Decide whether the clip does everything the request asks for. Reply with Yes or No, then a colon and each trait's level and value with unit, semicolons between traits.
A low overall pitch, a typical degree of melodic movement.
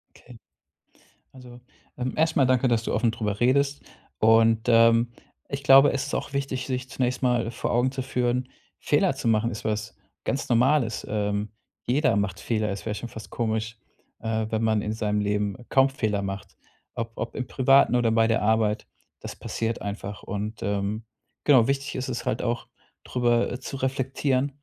Yes: low, 115 Hz; average, 3.0 semitones